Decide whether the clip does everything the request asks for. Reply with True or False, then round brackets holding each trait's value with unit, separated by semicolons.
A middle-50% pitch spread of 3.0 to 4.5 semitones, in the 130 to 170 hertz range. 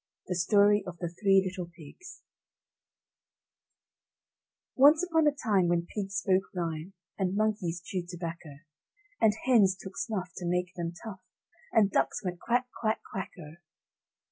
False (3.6 semitones; 190 Hz)